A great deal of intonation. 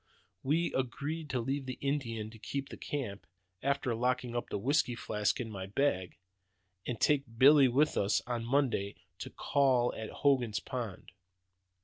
No: average, 3.6 semitones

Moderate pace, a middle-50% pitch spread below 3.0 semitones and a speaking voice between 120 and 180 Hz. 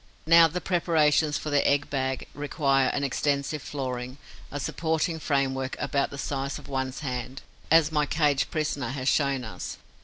Yes: average, 160 wpm; narrow, 2.4 semitones; medium, 140 Hz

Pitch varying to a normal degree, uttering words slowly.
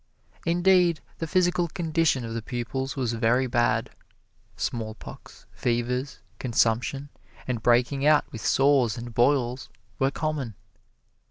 Yes: average, 4.0 semitones; slow, 115 wpm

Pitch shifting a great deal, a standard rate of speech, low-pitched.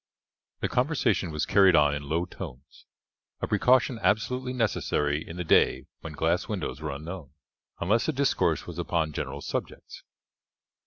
Yes: wide, 6.5 semitones; average, 150 wpm; very low, 85 Hz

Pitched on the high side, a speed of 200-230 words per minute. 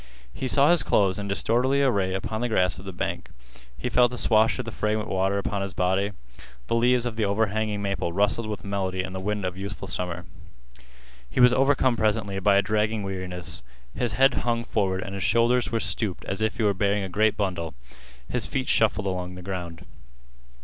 No: low, 100 Hz; fast, 205 wpm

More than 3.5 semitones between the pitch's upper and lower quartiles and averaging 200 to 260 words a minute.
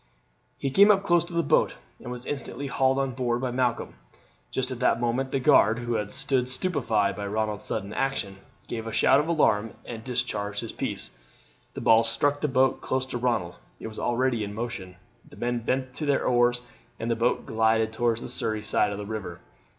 No: average, 3.1 semitones; fast, 205 wpm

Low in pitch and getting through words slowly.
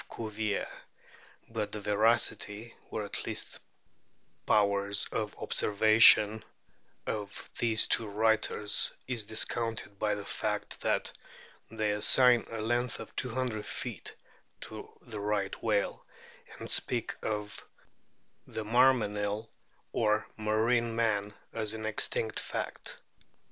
Yes: low, 110 Hz; slow, 110 wpm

